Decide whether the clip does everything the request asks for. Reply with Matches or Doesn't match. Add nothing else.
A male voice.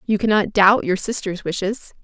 Doesn't match